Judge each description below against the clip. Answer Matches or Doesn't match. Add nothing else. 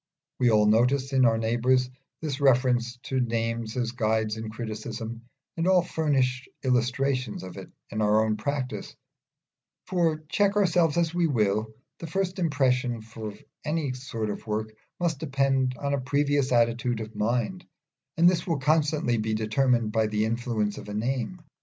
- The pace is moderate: Matches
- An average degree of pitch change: Matches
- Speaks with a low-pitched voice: Matches